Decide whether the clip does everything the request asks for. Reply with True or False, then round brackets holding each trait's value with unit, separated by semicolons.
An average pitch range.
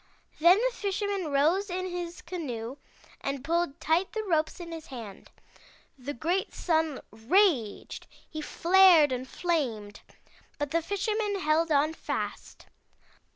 True (4.8 semitones)